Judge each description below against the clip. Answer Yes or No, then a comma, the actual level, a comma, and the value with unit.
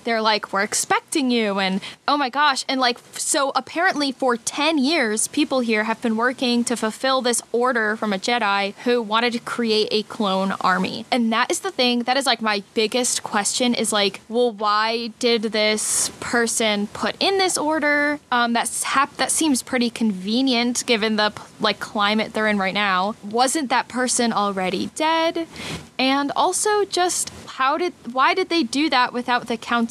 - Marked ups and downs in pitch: No, average, 4.0 semitones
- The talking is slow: No, average, 180 wpm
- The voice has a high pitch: Yes, high, 240 Hz